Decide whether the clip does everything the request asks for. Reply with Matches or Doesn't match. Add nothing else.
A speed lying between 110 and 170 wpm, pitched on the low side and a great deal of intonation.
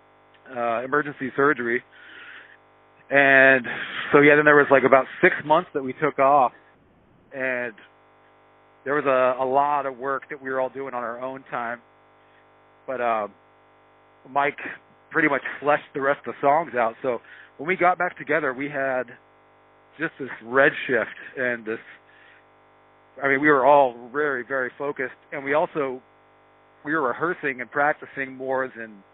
Matches